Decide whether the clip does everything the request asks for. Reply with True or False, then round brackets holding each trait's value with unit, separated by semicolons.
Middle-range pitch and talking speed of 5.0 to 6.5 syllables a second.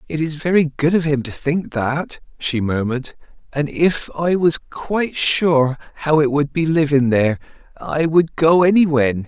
False (150 Hz; 4.5 syllables/s)